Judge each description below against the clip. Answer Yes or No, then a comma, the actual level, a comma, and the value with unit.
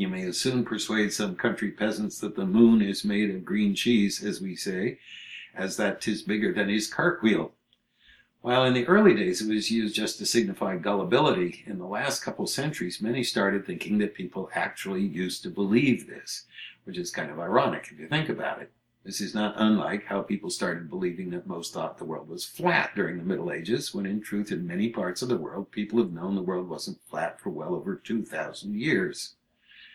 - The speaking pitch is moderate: No, low, 105 Hz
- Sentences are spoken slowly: No, fast, 205 wpm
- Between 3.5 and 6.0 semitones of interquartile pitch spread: No, average, 3.1 semitones